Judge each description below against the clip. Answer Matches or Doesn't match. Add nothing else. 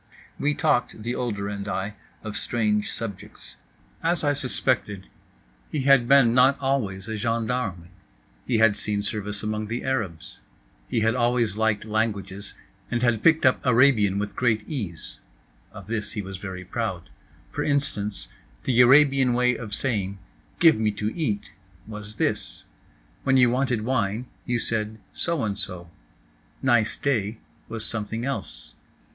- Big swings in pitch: Doesn't match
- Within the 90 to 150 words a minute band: Matches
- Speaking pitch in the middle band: Doesn't match